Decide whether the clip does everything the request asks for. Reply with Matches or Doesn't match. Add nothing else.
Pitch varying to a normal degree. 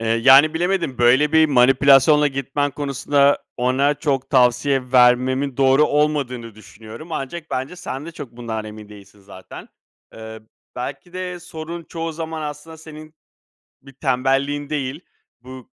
Matches